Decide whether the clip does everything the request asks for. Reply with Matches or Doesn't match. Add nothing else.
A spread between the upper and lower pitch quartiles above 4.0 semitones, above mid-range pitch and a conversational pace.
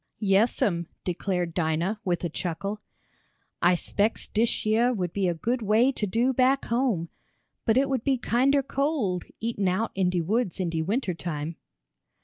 Matches